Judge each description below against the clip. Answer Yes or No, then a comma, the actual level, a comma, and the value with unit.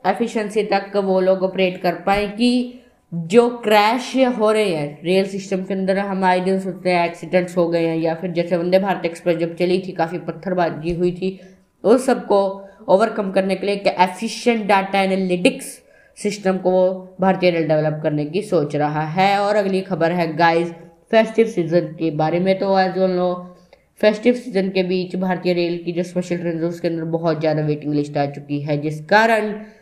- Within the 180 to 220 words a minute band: Yes, fast, 190 wpm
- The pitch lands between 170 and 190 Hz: Yes, medium, 185 Hz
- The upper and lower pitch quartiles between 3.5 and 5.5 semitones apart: No, average, 2.7 semitones